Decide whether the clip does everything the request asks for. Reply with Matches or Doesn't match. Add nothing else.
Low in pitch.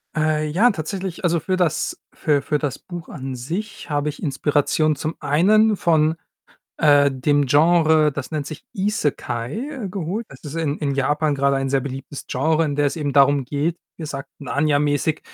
Doesn't match